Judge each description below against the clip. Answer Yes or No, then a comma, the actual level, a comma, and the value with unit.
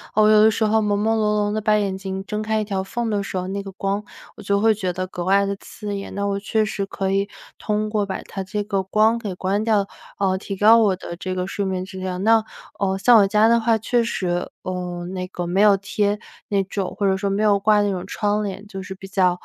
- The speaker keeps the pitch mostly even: Yes, narrow, 1.8 semitones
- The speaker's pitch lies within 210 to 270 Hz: No, high, 200 Hz